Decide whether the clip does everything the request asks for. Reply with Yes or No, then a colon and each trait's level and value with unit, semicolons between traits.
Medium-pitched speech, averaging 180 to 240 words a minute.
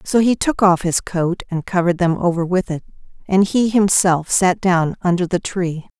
Yes: medium, 180 Hz; average, 200 wpm